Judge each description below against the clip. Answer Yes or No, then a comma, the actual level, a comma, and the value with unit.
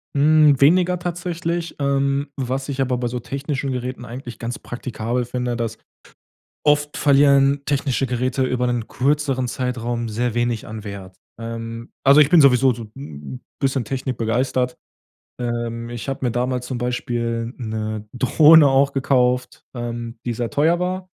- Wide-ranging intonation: No, average, 2.8 semitones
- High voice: No, low, 125 Hz